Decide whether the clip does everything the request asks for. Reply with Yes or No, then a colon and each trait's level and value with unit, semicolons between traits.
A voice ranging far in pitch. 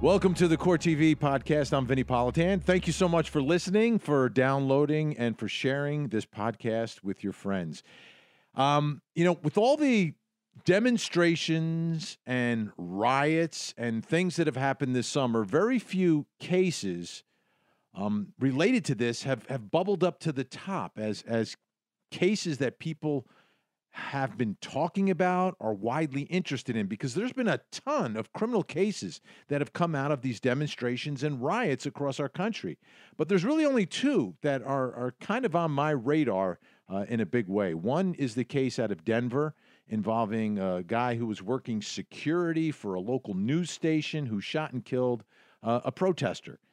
Yes: wide, 6.1 semitones